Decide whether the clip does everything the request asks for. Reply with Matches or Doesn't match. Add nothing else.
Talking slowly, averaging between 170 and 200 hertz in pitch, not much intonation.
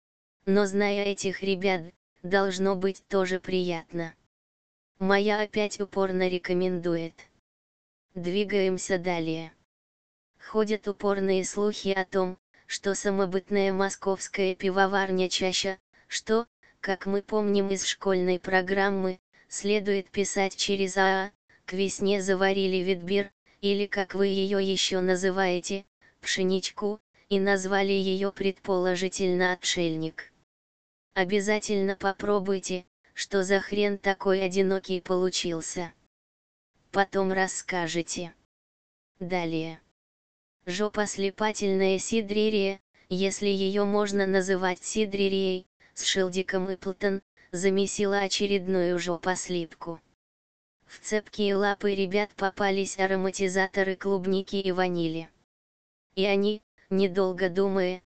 Matches